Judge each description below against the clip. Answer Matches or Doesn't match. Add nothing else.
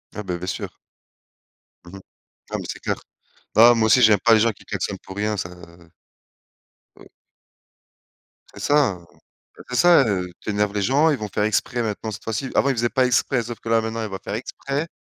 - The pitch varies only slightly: Doesn't match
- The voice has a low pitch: Matches